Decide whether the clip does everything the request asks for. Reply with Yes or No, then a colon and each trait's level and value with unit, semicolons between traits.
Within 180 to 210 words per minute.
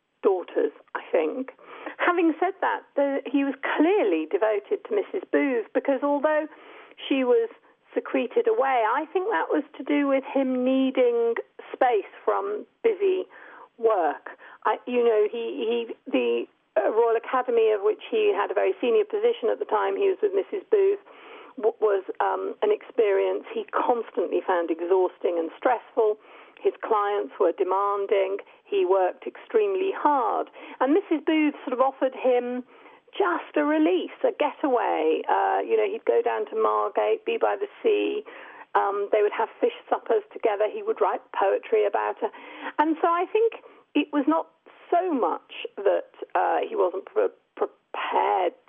No: average, 160 wpm